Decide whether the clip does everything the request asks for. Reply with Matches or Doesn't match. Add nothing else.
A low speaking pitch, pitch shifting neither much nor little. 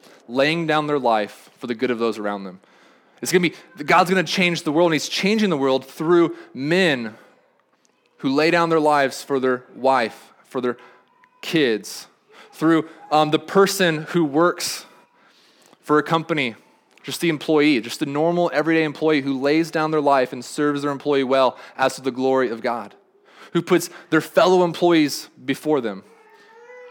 Doesn't match